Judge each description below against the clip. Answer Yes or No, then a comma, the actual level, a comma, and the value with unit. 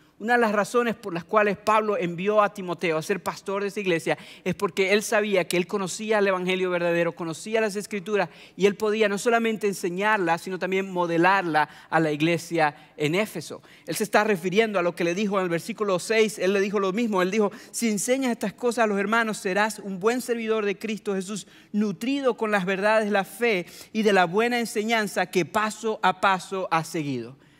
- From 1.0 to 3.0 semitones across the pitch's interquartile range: No, average, 3.4 semitones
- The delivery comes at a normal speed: No, fast, 210 wpm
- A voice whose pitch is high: Yes, high, 200 Hz